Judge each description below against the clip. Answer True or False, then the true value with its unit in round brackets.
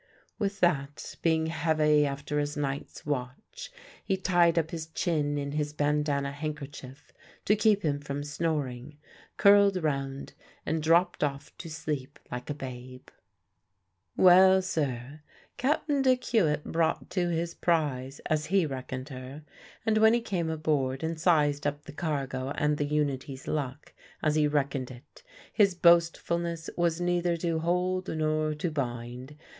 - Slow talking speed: False (145 wpm)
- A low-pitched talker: False (150 Hz)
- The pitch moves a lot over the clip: False (3.3 semitones)